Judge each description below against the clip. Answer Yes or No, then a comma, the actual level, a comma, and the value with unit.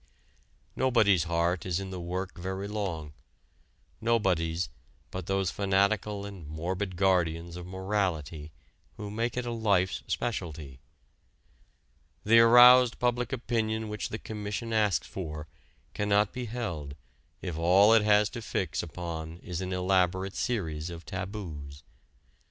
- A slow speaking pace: Yes, slow, 130 wpm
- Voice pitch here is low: Yes, very low, 95 Hz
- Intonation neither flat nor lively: Yes, average, 3.8 semitones